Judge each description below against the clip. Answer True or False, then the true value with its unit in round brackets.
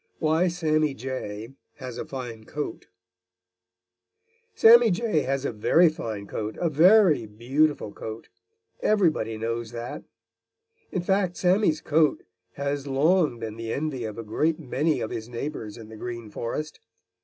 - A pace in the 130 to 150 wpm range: True (145 wpm)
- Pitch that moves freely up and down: True (5.9 semitones)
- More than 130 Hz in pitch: True (140 Hz)